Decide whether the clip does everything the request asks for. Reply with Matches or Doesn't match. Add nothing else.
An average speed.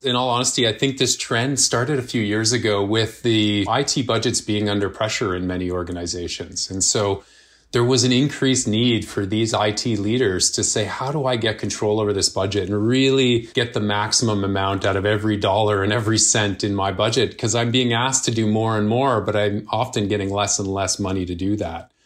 Doesn't match